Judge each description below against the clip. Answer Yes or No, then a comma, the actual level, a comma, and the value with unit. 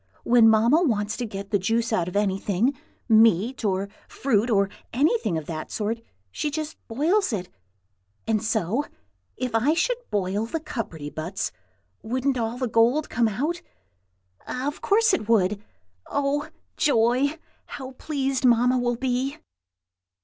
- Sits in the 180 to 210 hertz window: No, high, 235 Hz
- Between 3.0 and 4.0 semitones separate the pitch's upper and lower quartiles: No, average, 4.6 semitones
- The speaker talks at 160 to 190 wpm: No, average, 140 wpm